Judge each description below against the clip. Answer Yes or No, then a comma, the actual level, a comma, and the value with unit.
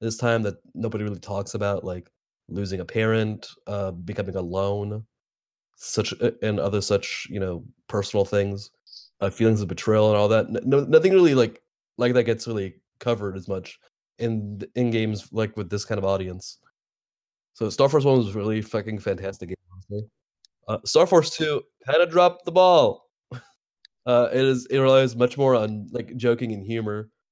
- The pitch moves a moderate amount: Yes, average, 3.4 semitones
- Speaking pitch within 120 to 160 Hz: No, low, 110 Hz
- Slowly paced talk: No, average, 170 wpm